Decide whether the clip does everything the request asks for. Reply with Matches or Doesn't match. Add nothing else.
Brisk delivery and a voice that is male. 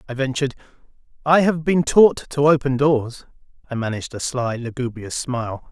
Doesn't match